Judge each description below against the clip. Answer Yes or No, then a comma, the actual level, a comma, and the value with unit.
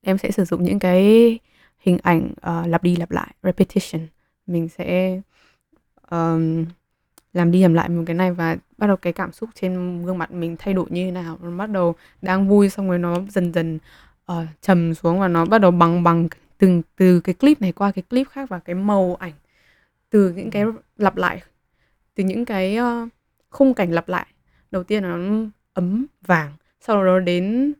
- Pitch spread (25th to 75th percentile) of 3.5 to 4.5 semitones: No, average, 2.7 semitones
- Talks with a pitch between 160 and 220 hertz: Yes, medium, 185 Hz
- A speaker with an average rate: Yes, average, 200 wpm